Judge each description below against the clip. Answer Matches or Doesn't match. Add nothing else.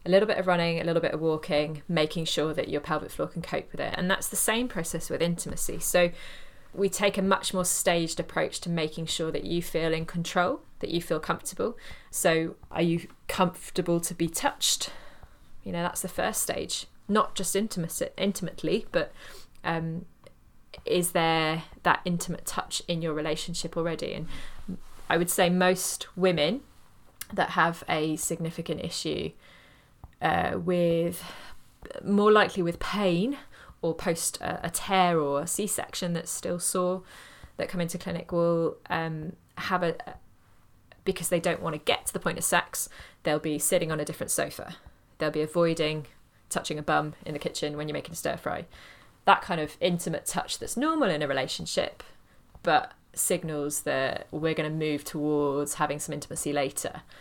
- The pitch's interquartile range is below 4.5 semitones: Matches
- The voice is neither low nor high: Matches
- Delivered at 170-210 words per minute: Matches